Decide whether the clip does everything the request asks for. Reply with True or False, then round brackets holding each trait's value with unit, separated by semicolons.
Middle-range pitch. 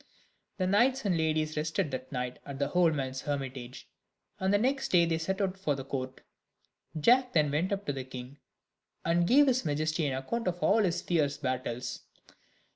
True (155 Hz)